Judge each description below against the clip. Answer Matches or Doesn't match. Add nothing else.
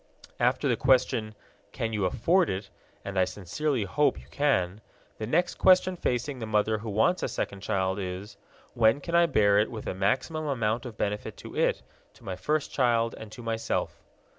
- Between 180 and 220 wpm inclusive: Matches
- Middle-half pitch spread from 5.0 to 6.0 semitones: Matches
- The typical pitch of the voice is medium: Doesn't match